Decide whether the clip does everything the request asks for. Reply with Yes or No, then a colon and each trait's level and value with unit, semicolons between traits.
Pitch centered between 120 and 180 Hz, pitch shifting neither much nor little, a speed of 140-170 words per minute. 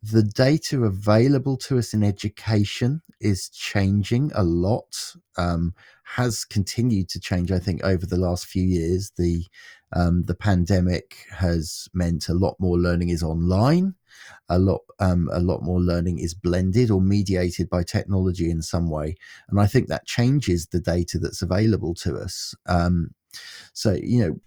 No: very low, 95 Hz; average, 3.5 semitones; average, 160 wpm